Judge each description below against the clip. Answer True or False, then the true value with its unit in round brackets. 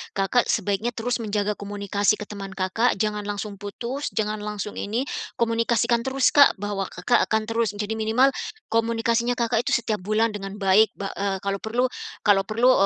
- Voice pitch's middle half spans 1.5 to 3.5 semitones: True (2.4 semitones)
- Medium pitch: False (215 Hz)